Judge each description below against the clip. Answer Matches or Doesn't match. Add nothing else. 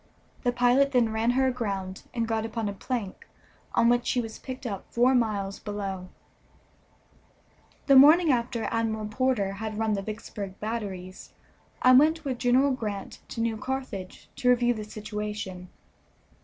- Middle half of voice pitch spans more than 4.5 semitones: Doesn't match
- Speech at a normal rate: Matches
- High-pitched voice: Matches